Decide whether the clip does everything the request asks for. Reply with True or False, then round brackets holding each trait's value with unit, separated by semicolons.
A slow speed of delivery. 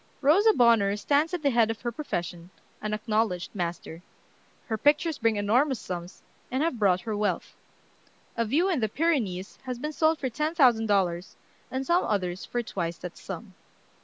False (175 wpm)